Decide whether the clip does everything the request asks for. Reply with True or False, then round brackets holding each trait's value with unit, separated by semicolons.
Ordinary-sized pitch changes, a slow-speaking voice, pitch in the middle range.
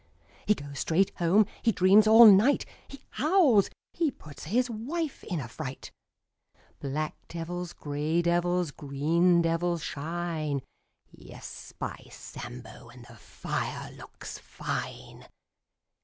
False (6.2 semitones; 125 wpm; 170 Hz)